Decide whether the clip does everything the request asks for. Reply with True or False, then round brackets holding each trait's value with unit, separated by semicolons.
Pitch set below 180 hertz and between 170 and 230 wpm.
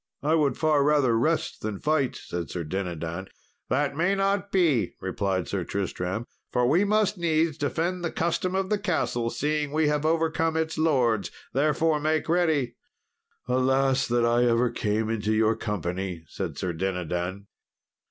False (135 Hz; 155 wpm)